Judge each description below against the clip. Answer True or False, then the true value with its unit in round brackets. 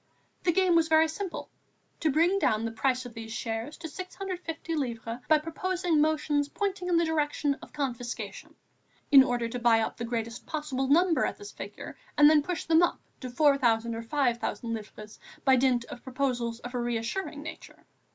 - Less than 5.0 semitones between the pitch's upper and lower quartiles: False (5.3 semitones)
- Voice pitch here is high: True (275 Hz)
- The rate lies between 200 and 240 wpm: False (180 wpm)